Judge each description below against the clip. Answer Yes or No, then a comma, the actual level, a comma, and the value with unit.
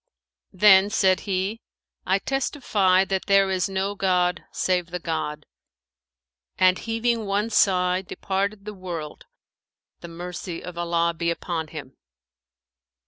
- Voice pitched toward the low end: No, medium, 185 Hz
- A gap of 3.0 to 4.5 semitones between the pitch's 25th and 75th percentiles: No, narrow, 2.4 semitones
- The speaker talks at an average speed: No, slow, 125 wpm